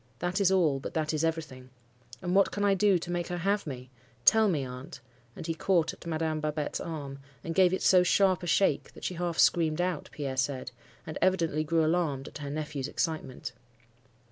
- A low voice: No, medium, 160 Hz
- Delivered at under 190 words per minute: No, fast, 205 wpm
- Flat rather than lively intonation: No, average, 3.4 semitones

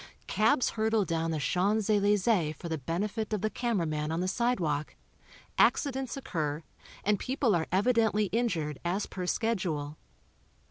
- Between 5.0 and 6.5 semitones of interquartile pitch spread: Yes, wide, 5.4 semitones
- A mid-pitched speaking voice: No, high, 195 Hz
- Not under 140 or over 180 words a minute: Yes, average, 145 wpm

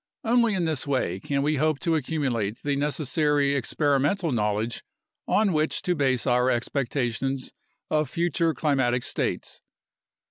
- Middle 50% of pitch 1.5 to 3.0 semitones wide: No, average, 3.7 semitones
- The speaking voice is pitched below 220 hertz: Yes, medium, 140 Hz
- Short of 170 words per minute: Yes, slow, 135 wpm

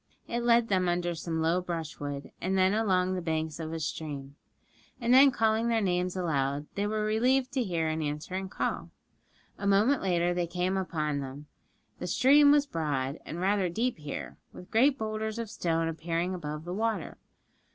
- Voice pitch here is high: No, medium, 180 Hz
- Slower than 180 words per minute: No, average, 185 wpm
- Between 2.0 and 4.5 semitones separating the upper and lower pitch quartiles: No, average, 5.2 semitones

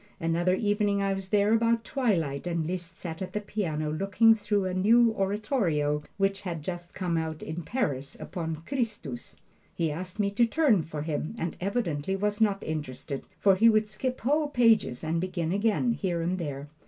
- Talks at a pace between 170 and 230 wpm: Yes, average, 180 wpm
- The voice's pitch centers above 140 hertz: Yes, high, 190 Hz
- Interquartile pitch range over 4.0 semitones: Yes, average, 4.8 semitones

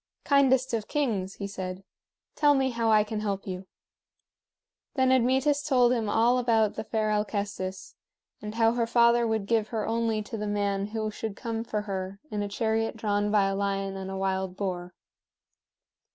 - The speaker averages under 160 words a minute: No, average, 180 wpm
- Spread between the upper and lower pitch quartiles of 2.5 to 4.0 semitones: Yes, average, 2.8 semitones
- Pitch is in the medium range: No, high, 215 Hz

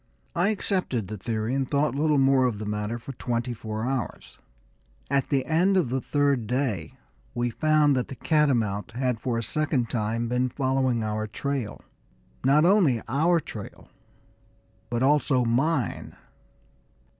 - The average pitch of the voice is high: No, low, 130 Hz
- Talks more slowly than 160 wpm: Yes, average, 150 wpm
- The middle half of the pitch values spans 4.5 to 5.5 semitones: No, average, 3.8 semitones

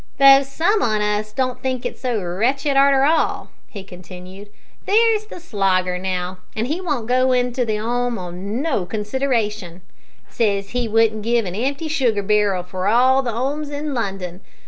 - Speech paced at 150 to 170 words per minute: Yes, average, 165 wpm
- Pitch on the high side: Yes, high, 230 Hz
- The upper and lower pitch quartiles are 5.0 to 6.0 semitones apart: Yes, wide, 5.4 semitones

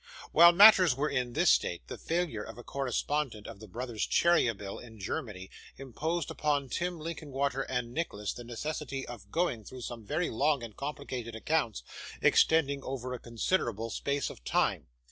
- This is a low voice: Yes, low, 130 Hz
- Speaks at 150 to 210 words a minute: Yes, average, 165 wpm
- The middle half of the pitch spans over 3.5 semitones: Yes, average, 4.8 semitones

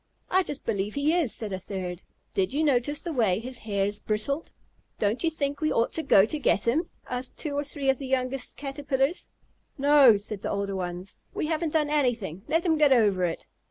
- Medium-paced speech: No, fast, 210 wpm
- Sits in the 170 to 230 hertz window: No, very high, 260 Hz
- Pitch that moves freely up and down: Yes, wide, 6.3 semitones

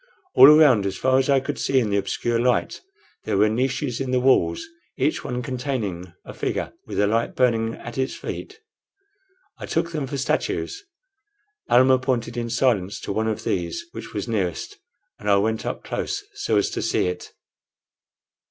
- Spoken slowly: No, average, 180 wpm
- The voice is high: No, low, 120 Hz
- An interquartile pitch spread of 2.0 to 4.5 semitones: Yes, average, 3.9 semitones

